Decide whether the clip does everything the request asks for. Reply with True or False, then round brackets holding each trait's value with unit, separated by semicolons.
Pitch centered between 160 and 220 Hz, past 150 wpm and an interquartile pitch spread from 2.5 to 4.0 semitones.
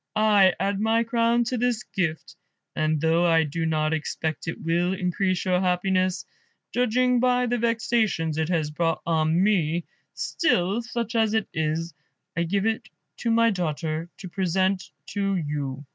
False (185 Hz; 160 wpm; 5.3 semitones)